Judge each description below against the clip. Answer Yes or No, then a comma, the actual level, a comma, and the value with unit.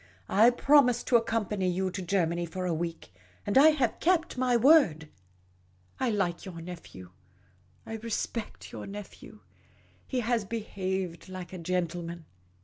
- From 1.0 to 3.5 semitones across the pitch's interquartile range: No, average, 5.2 semitones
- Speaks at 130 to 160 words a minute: Yes, average, 140 wpm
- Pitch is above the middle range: Yes, high, 195 Hz